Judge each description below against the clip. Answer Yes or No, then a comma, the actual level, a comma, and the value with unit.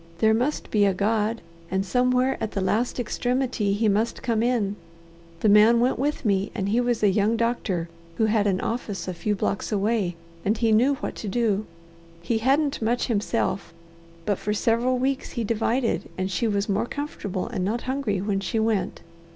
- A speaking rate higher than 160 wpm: Yes, average, 190 wpm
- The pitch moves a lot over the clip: No, average, 3.2 semitones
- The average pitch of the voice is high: Yes, high, 220 Hz